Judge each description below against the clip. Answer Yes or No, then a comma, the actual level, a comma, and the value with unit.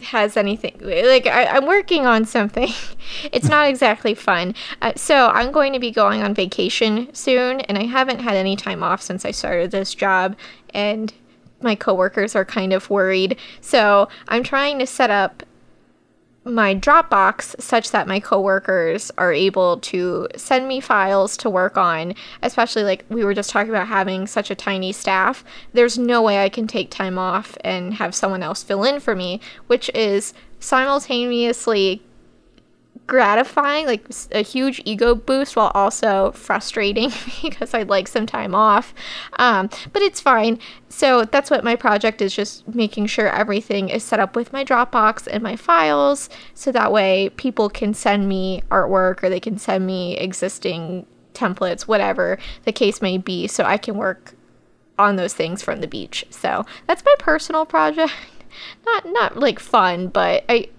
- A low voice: No, high, 215 Hz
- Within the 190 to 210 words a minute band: No, average, 170 wpm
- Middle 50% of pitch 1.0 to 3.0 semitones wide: No, average, 4.5 semitones